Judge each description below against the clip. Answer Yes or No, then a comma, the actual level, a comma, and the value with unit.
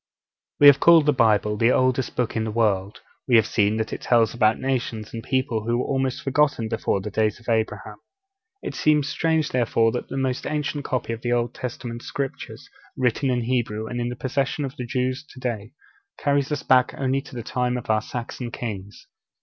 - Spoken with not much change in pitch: No, average, 3.0 semitones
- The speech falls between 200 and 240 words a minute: Yes, fast, 205 wpm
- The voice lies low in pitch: Yes, low, 120 Hz